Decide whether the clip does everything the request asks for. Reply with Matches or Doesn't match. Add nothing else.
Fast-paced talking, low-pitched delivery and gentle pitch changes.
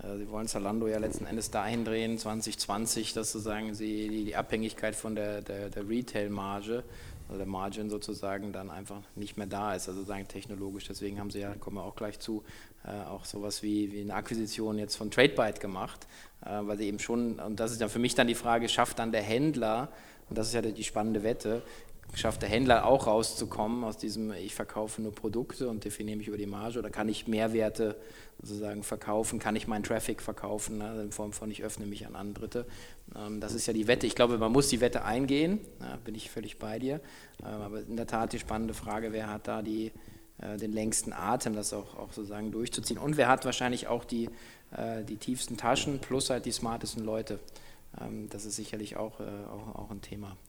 Matches